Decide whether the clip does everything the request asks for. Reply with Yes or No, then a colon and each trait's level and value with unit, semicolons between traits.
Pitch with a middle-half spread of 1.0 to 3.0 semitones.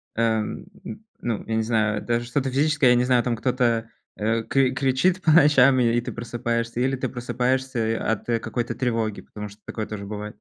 Yes: narrow, 2.6 semitones